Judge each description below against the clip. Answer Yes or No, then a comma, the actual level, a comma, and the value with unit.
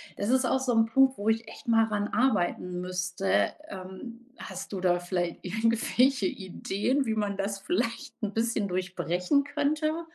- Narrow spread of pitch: No, average, 5.1 semitones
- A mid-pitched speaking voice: No, high, 210 Hz